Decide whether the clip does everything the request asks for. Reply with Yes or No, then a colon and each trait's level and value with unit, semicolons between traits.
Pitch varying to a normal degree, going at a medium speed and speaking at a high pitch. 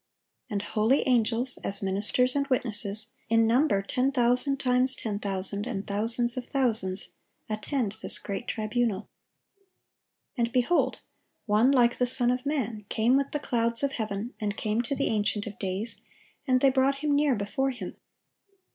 Yes: average, 3.6 semitones; average, 160 wpm; high, 235 Hz